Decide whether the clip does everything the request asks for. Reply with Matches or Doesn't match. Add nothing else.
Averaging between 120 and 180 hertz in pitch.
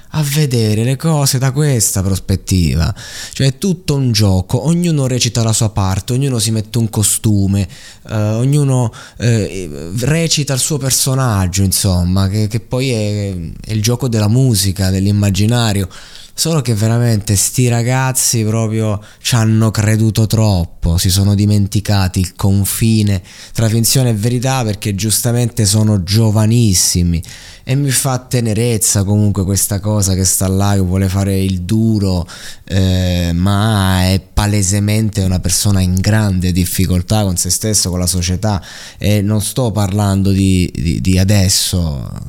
Doesn't match